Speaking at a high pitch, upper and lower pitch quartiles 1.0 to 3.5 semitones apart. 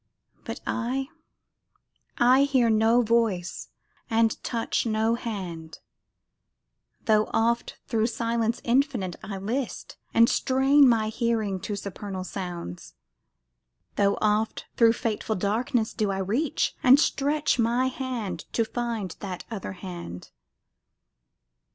Yes: high, 225 Hz; average, 3.2 semitones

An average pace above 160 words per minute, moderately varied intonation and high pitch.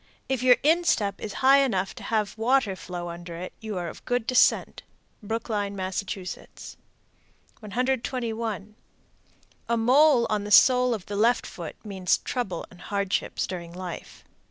No: average, 145 wpm; average, 4.7 semitones; high, 215 Hz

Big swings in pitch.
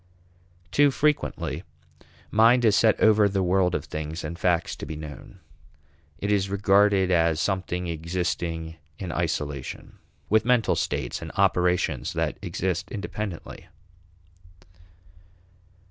No: average, 3.9 semitones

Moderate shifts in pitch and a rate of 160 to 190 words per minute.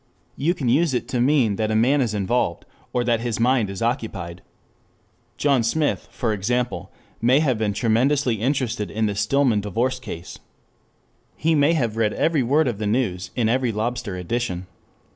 Yes: average, 3.6 semitones; average, 175 wpm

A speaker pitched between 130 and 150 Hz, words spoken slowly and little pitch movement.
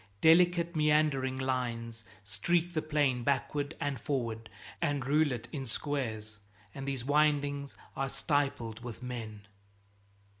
No: low, 135 Hz; slow, 120 wpm; average, 3.8 semitones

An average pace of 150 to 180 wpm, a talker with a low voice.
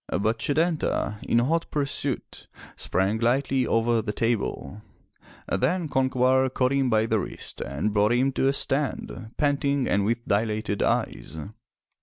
No: average, 140 wpm; low, 120 Hz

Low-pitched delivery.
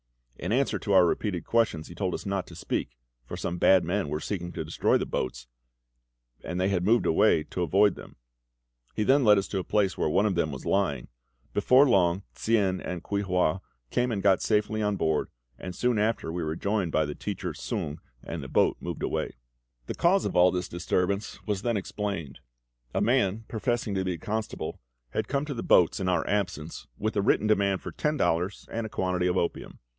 Yes: very low, 95 Hz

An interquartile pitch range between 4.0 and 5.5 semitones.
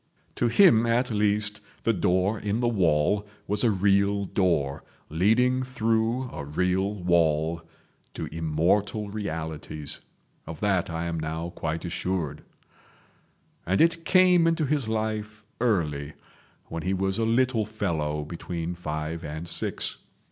Yes: average, 5.2 semitones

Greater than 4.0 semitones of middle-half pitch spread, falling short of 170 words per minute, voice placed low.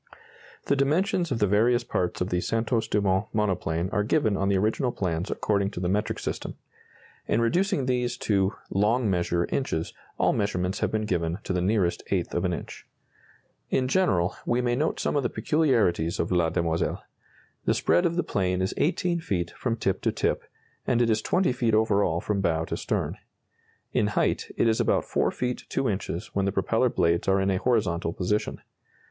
No: average, 5.1 semitones; average, 195 wpm; low, 105 Hz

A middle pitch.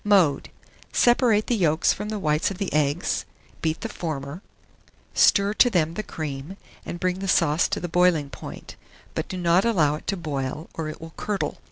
Yes: medium, 170 Hz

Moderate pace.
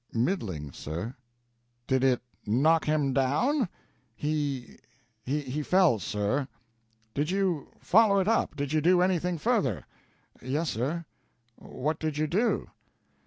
No: slow, 120 wpm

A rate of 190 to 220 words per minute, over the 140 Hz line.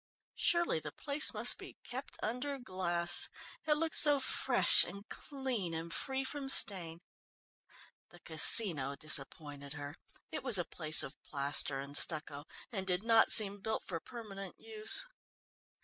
No: average, 145 wpm; high, 190 Hz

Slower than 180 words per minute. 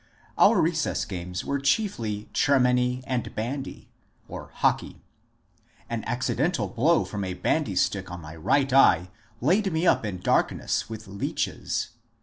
Yes: average, 140 wpm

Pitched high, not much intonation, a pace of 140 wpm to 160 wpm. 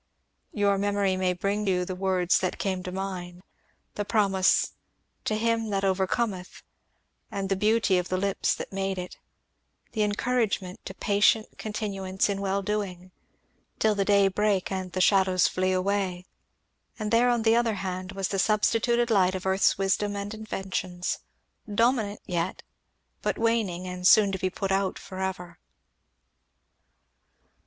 Yes: high, 195 Hz; narrow, 2.0 semitones; average, 155 wpm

